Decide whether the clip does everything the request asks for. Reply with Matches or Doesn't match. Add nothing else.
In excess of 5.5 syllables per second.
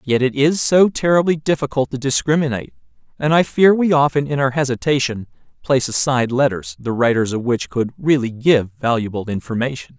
Matches